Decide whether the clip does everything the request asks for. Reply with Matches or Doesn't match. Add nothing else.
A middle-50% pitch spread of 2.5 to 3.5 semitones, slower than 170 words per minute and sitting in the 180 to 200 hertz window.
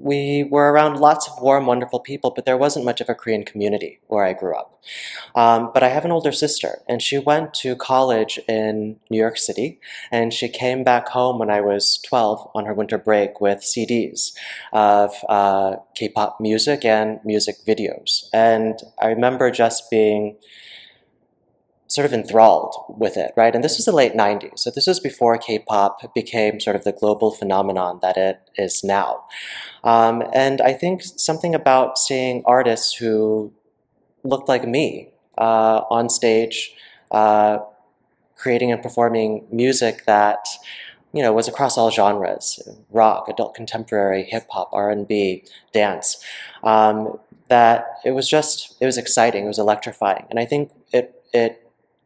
Doesn't match